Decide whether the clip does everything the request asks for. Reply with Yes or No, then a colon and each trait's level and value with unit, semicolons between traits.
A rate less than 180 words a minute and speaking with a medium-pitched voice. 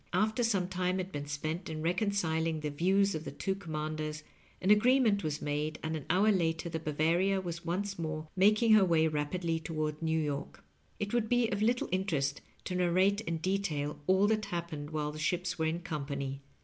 No: average, 195 wpm; medium, 170 Hz